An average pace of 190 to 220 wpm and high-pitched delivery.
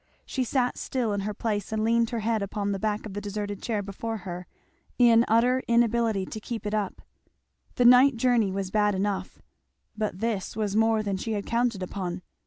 Yes: average, 195 wpm; high, 215 Hz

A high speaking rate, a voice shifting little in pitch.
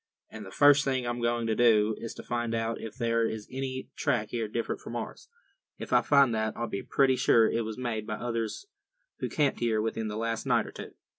Yes: fast, 230 wpm; narrow, 1.9 semitones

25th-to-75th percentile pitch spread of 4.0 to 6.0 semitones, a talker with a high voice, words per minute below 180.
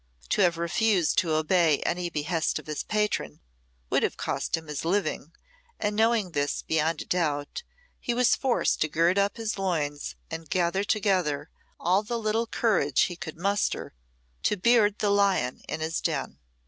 No: average, 4.7 semitones; medium, 180 Hz; average, 170 wpm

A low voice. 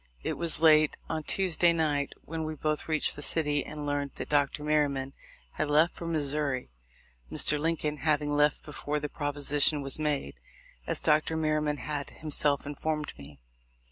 No: medium, 150 Hz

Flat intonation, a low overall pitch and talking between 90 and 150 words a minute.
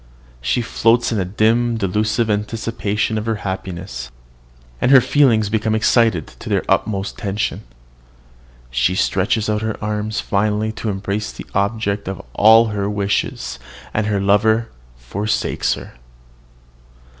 Yes: narrow, 2.0 semitones; low, 105 Hz; slow, 135 wpm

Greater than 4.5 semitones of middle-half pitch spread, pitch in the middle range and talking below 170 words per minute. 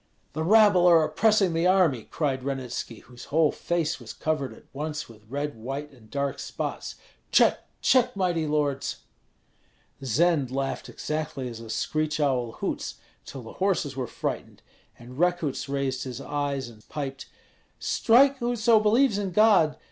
Yes: average, 5.1 semitones; medium, 150 Hz; average, 150 wpm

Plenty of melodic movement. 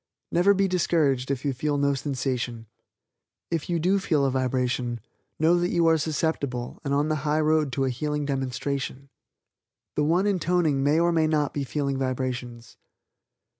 No: average, 3.5 semitones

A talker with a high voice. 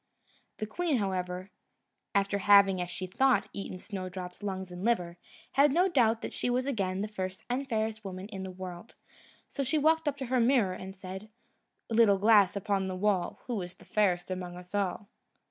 Yes: high, 200 Hz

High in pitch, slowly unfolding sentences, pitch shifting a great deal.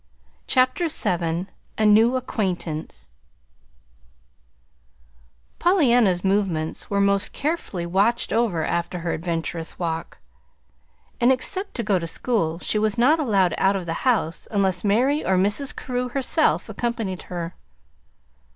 Yes: high, 200 Hz; slow, 125 wpm; wide, 6.0 semitones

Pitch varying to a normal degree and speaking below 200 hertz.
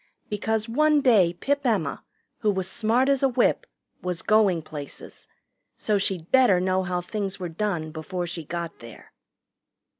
Yes: average, 4.4 semitones; high, 190 Hz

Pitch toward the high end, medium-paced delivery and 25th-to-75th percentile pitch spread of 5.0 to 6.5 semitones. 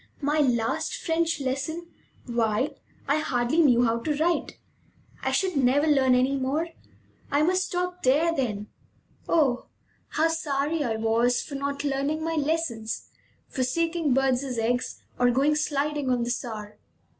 No: very high, 280 Hz; average, 145 wpm; average, 4.2 semitones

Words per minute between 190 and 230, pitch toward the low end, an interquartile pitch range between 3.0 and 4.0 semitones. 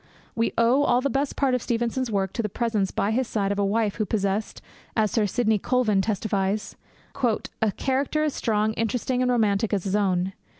No: average, 200 wpm; high, 220 Hz; average, 3.5 semitones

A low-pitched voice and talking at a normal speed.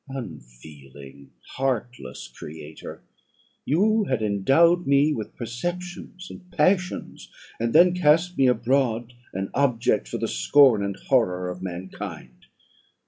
No: low, 125 Hz; slow, 115 wpm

